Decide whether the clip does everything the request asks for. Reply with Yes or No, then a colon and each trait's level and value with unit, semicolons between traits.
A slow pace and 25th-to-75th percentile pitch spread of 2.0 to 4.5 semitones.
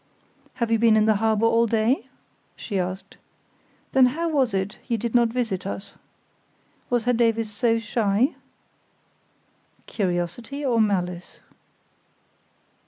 Yes: slow, 125 wpm; average, 3.1 semitones